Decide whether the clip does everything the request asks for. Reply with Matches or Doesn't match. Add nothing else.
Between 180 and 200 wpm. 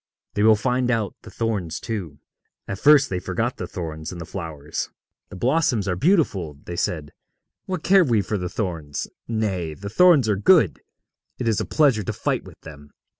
Matches